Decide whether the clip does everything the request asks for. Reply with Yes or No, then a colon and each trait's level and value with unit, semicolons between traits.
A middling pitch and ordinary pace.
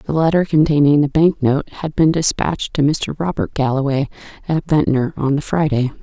Yes: medium, 145 Hz; average, 180 wpm